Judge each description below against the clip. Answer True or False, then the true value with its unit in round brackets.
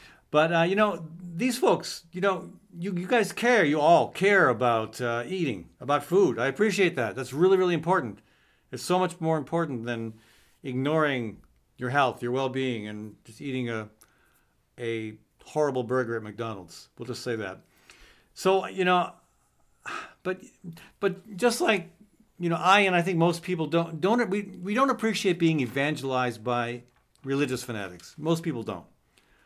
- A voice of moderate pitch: True (155 Hz)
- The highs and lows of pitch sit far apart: True (7.2 semitones)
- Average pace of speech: True (165 wpm)